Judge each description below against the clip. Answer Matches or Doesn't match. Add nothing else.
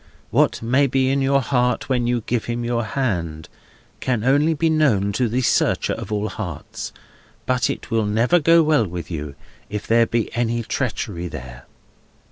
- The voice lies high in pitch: Doesn't match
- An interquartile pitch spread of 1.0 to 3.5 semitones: Doesn't match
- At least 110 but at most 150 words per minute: Doesn't match